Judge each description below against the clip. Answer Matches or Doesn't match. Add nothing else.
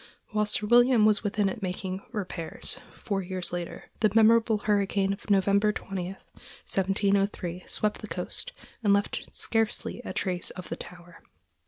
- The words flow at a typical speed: Matches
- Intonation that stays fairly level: Matches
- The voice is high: Matches